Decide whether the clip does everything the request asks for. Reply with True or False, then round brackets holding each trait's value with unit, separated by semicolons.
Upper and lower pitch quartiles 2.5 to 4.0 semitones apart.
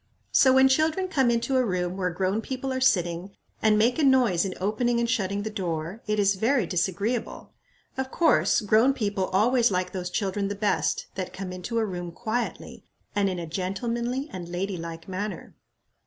False (4.7 semitones)